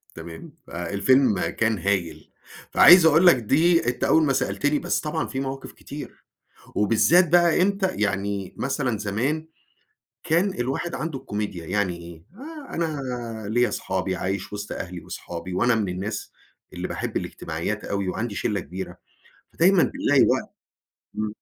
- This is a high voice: No, low, 120 Hz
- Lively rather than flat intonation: Yes, wide, 8.2 semitones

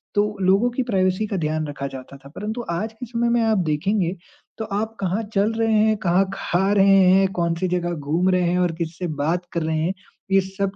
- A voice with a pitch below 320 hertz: Yes, high, 190 Hz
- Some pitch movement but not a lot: Yes, average, 3.7 semitones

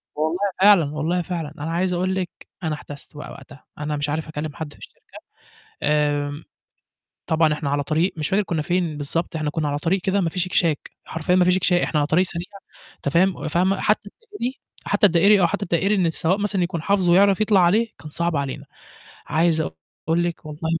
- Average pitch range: Yes, average, 3.6 semitones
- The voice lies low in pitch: No, medium, 170 Hz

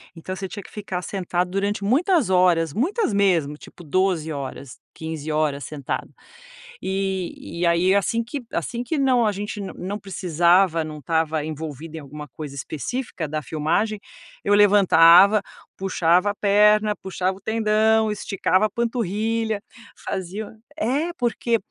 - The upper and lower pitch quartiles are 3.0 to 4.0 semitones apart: No, average, 4.7 semitones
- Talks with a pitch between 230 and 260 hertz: No, high, 190 Hz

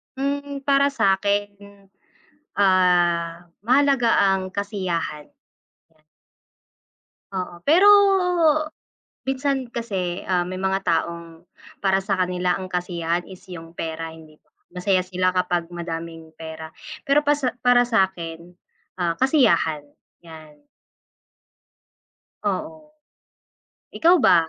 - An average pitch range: No, wide, 6.3 semitones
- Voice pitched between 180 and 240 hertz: Yes, medium, 185 Hz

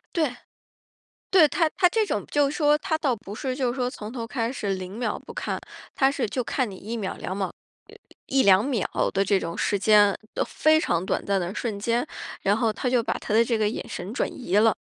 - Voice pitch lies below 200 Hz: No, high, 230 Hz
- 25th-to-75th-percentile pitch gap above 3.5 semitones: Yes, average, 5.1 semitones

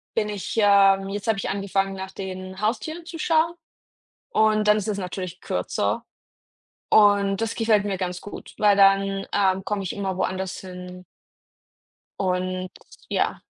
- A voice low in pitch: No, high, 195 Hz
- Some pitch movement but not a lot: No, narrow, 1.8 semitones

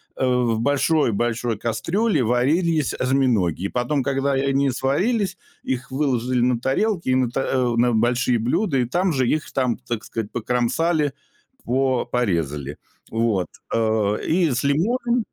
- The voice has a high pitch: No, low, 130 Hz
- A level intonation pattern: No, average, 3.8 semitones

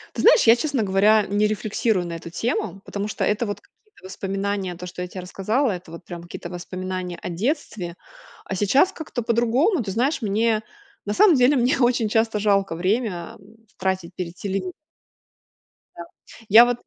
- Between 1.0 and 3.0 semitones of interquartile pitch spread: No, average, 4.2 semitones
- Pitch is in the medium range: No, high, 205 Hz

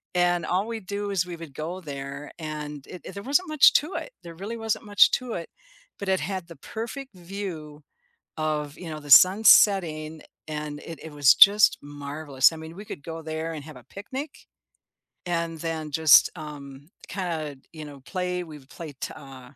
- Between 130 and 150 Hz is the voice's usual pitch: No, medium, 165 Hz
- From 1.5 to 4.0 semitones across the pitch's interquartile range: No, average, 4.4 semitones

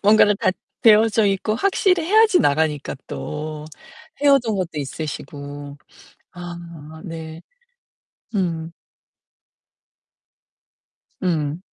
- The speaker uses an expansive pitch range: Yes, wide, 6.0 semitones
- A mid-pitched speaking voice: Yes, medium, 170 Hz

